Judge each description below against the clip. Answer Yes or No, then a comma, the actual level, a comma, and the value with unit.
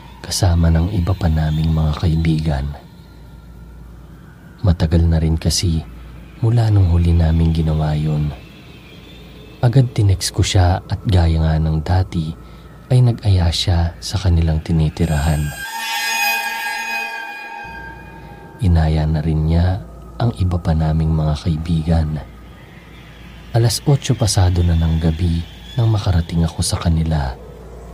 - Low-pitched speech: Yes, very low, 85 Hz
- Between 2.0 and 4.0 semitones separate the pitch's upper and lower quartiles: Yes, average, 2.8 semitones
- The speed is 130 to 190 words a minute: No, average, 115 wpm